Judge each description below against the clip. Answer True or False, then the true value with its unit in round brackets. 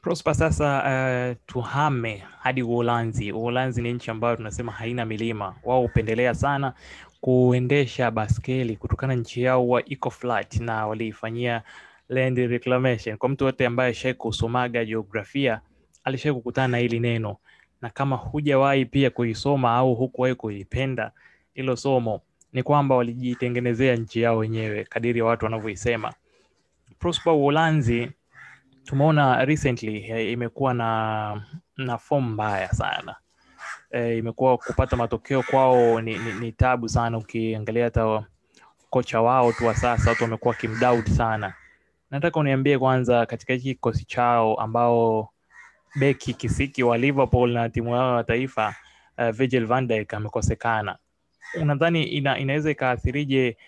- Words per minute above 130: False (115 wpm)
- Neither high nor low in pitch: False (120 Hz)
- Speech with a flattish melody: True (2.3 semitones)